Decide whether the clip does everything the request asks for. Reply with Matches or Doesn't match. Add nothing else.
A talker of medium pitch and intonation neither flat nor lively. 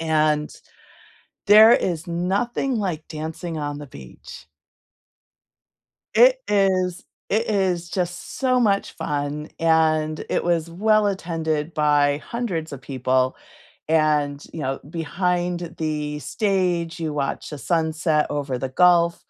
Matches